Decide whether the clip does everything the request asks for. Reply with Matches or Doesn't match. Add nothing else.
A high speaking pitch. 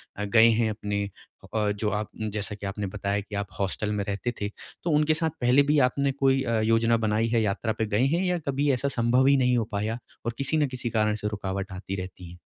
Doesn't match